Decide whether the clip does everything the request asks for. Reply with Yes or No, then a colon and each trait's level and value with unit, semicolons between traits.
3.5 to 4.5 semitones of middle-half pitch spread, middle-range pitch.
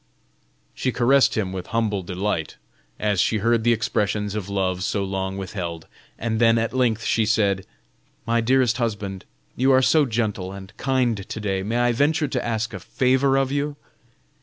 No: average, 3.9 semitones; low, 110 Hz